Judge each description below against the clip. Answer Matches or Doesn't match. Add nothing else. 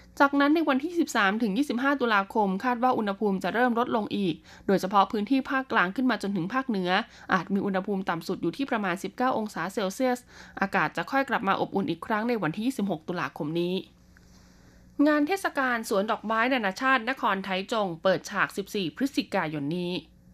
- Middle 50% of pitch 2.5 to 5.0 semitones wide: Doesn't match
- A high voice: Matches